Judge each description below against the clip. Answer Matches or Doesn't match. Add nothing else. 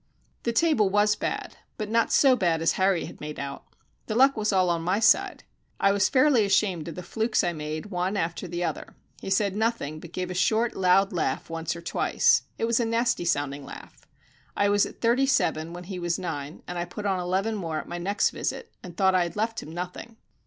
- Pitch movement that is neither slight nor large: Matches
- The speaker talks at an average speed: Doesn't match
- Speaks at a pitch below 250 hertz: Matches